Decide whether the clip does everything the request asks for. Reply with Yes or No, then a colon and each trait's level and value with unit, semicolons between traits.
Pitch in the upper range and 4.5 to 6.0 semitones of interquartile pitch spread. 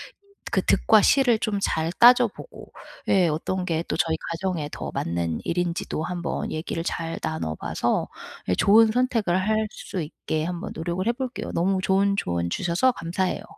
No: medium, 180 Hz; average, 4.8 semitones